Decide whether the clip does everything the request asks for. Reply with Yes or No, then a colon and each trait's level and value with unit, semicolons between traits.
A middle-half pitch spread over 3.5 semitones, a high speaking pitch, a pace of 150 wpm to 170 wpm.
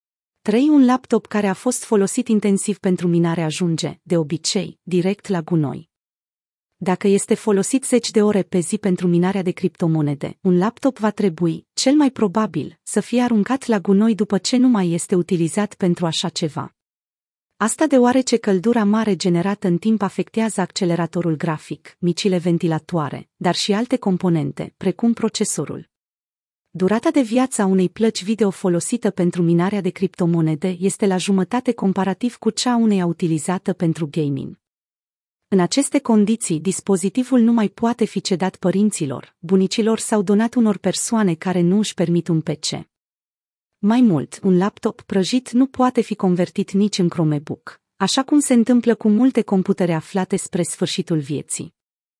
Yes: average, 4.2 semitones; high, 195 Hz; average, 155 wpm